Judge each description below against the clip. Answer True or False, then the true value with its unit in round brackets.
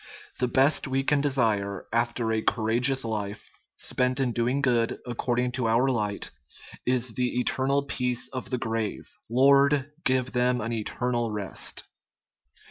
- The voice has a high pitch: False (125 Hz)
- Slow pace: False (145 wpm)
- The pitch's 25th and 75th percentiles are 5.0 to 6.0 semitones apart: False (2.4 semitones)